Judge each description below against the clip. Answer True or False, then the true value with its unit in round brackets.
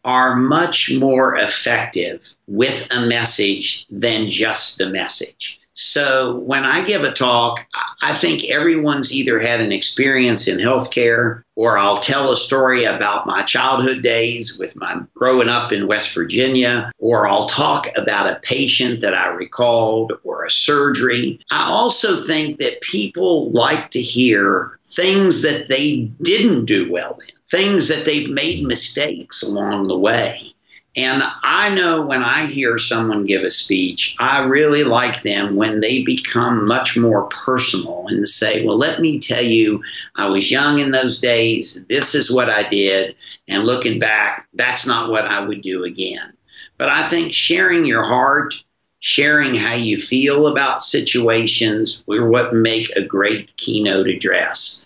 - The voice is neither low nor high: False (120 Hz)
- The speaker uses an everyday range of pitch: True (3.5 semitones)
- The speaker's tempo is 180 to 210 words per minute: False (160 wpm)